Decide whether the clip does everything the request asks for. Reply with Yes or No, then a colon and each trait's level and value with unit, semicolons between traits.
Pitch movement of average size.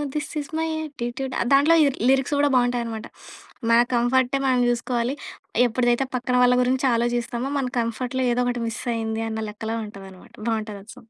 No: narrow, 2.3 semitones